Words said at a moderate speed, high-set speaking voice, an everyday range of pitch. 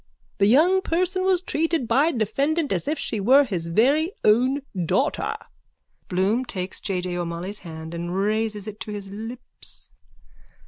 No: average, 150 wpm; high, 220 Hz; wide, 7.2 semitones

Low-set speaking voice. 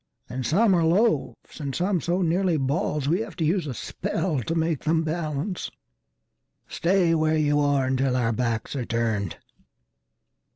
No: medium, 155 Hz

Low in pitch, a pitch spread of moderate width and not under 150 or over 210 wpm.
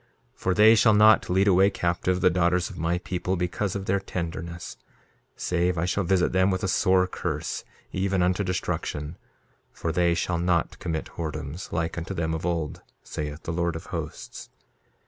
No: very low, 90 Hz; narrow, 1.9 semitones; average, 180 wpm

